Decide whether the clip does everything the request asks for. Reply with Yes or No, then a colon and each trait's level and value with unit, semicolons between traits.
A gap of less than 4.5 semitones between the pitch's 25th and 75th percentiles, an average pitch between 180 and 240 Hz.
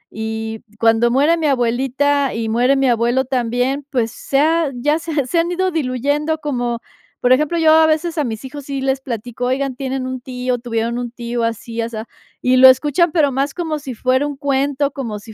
No: average, 3.3 semitones; very high, 260 Hz